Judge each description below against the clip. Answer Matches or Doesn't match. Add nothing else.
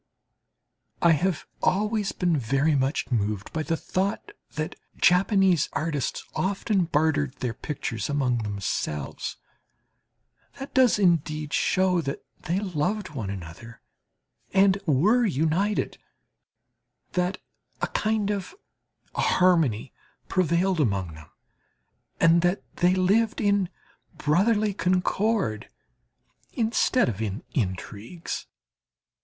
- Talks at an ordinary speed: Doesn't match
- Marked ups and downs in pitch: Matches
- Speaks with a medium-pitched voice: Matches